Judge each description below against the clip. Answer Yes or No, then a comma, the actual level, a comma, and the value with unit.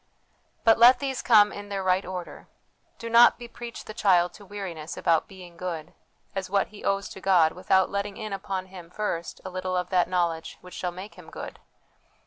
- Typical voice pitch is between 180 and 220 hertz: Yes, high, 190 Hz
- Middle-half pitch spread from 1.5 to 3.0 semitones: Yes, narrow, 2.5 semitones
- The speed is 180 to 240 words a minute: Yes, average, 195 wpm